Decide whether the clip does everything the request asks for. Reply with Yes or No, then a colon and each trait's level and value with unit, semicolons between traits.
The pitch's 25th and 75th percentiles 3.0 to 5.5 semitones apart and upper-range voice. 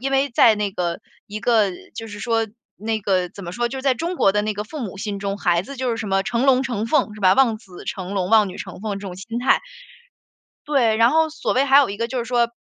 Yes: average, 3.9 semitones; high, 220 Hz